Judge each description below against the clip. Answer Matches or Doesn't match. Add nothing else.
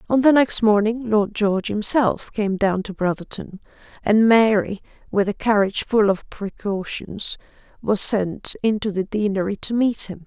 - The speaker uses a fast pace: Doesn't match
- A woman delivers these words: Matches